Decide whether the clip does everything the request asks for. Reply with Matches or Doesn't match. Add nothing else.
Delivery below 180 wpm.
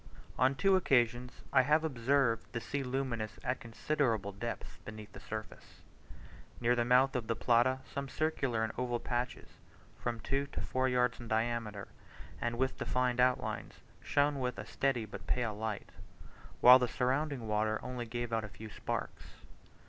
Matches